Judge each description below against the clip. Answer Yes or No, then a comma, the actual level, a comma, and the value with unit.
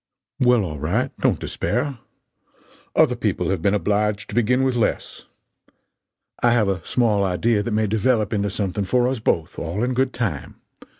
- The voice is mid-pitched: No, low, 105 Hz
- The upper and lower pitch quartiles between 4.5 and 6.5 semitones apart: No, average, 3.7 semitones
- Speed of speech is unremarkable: Yes, average, 170 wpm